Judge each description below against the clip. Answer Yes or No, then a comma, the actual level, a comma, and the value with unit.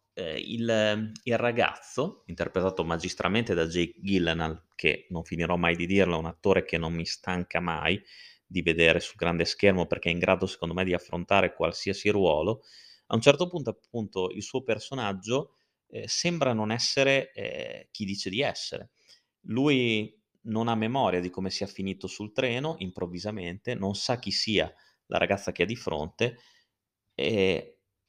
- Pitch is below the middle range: Yes, low, 100 Hz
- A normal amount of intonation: Yes, average, 4.7 semitones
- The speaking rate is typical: Yes, average, 160 wpm